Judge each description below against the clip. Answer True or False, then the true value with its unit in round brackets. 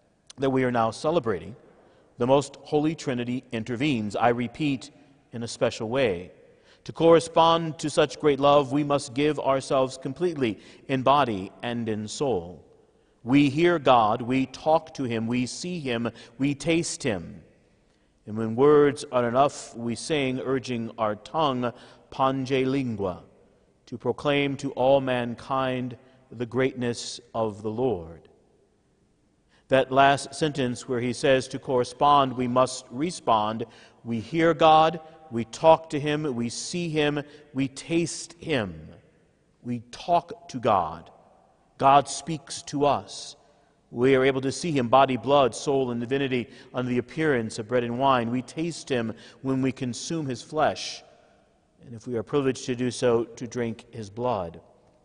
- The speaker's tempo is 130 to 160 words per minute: True (150 wpm)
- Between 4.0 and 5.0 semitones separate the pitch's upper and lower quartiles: False (3.3 semitones)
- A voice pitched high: False (130 Hz)